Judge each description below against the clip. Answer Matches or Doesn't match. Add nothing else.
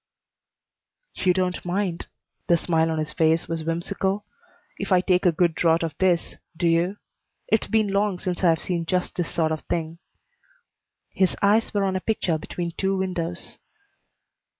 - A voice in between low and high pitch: Matches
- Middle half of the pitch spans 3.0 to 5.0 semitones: Doesn't match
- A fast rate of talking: Doesn't match